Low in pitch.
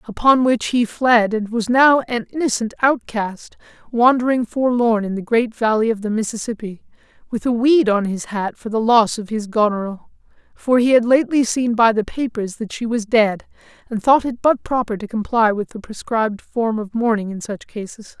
No: high, 230 Hz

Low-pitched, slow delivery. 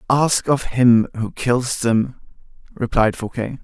Yes: low, 120 Hz; slow, 130 wpm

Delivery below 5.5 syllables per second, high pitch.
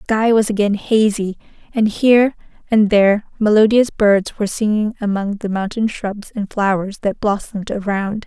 Yes: 5.0 syllables/s; high, 210 Hz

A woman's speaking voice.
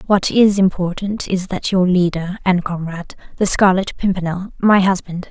Yes: female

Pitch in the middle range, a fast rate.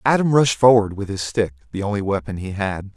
No: low, 105 Hz; fast, 225 wpm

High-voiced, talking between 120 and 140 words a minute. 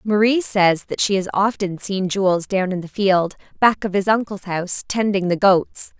No: high, 195 Hz; average, 200 wpm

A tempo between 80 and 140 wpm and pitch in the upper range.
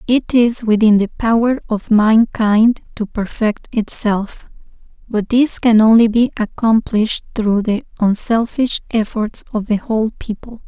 Yes: slow, 135 wpm; high, 220 Hz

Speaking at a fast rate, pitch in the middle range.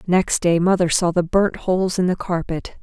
Yes: fast, 210 wpm; medium, 180 Hz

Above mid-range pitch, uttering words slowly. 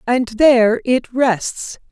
Yes: very high, 250 Hz; slow, 125 wpm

